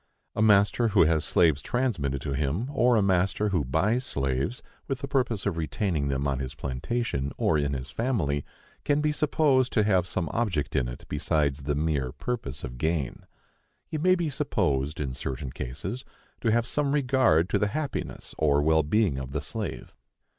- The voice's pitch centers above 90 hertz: No, very low, 85 Hz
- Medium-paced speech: Yes, average, 185 wpm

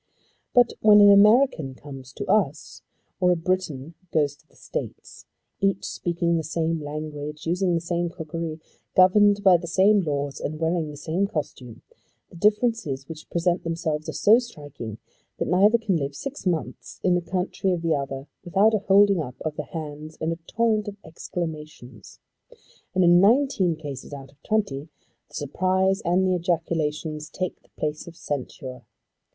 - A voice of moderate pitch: Yes, medium, 170 Hz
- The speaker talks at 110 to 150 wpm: No, average, 170 wpm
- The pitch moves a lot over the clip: No, average, 4.2 semitones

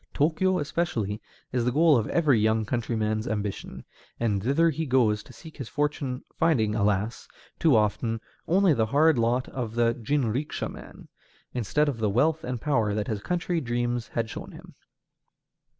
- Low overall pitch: Yes, low, 120 Hz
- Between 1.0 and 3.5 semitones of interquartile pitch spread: No, average, 5.2 semitones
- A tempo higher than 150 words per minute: Yes, average, 165 wpm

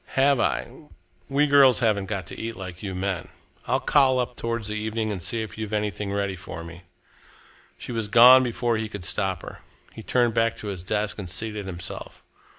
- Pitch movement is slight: No, average, 3.3 semitones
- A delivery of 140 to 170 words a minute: No, average, 200 wpm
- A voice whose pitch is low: Yes, low, 105 Hz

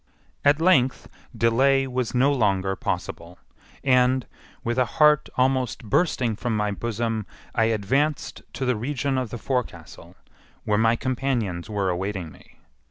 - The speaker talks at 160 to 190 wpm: No, average, 140 wpm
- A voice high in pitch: No, low, 120 Hz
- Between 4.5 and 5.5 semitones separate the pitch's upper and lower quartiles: No, average, 4.0 semitones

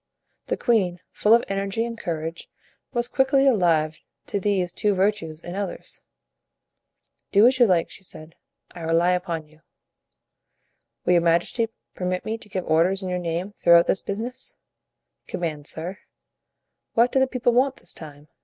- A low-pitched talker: No, medium, 185 Hz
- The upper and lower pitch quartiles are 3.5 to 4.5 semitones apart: No, average, 5.0 semitones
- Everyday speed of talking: Yes, average, 160 wpm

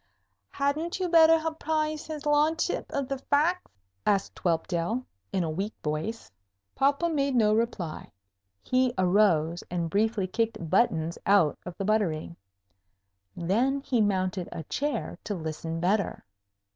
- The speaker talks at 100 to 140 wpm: Yes, slow, 135 wpm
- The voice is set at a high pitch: Yes, high, 215 Hz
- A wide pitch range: Yes, wide, 8.2 semitones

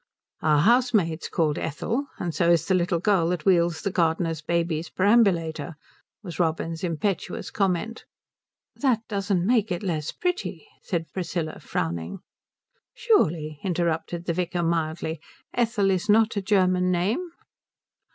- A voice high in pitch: No, medium, 175 Hz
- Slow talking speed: Yes, slow, 130 wpm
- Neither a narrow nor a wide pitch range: Yes, average, 3.7 semitones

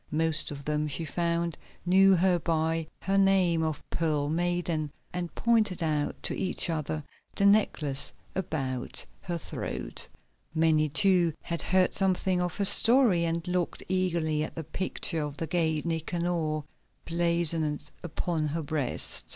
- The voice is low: No, medium, 165 Hz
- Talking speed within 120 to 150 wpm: Yes, average, 145 wpm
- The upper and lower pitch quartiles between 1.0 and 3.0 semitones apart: Yes, narrow, 2.6 semitones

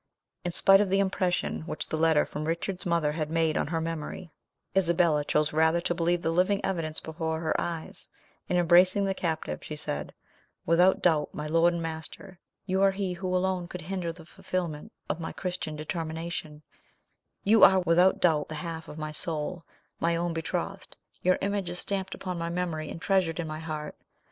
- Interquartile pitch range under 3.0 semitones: Yes, narrow, 2.4 semitones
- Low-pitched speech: No, medium, 170 Hz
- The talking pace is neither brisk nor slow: Yes, average, 190 wpm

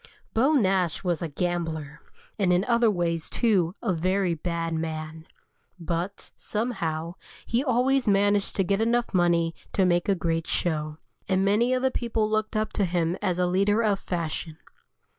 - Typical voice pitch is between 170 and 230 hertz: Yes, medium, 185 Hz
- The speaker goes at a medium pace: Yes, average, 165 wpm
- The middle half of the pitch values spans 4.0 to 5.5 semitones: Yes, average, 4.3 semitones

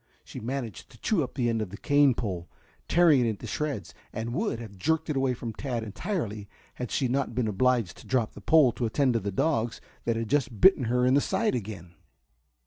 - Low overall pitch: Yes, low, 120 Hz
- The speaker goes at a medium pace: No, fast, 225 wpm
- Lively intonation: No, average, 4.2 semitones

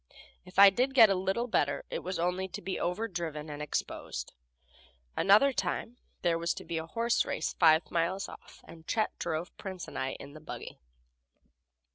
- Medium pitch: Yes, medium, 180 Hz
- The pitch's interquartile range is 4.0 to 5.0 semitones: No, average, 3.5 semitones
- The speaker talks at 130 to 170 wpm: No, average, 180 wpm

